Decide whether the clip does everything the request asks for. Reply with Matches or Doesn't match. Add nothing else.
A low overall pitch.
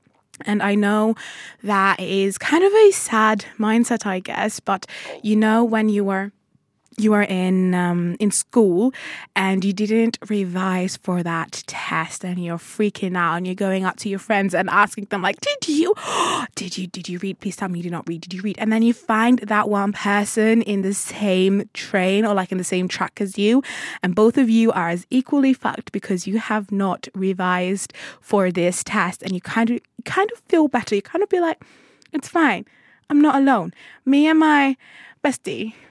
Doesn't match